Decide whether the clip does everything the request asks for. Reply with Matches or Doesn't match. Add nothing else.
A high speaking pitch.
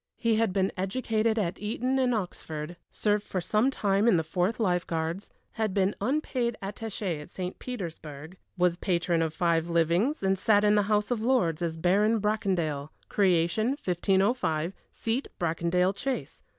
Matches